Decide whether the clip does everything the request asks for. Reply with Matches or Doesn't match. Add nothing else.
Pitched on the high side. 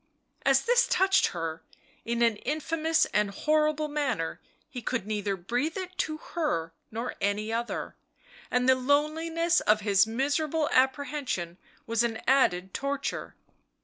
Matches